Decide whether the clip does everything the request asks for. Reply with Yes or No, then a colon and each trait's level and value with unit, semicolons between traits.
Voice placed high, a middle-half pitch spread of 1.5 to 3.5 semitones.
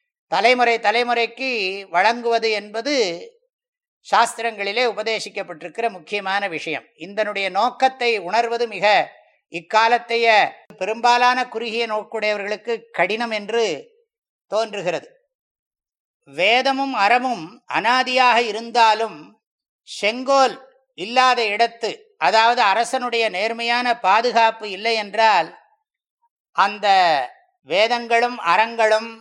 Yes: high, 230 Hz; average, 2.9 semitones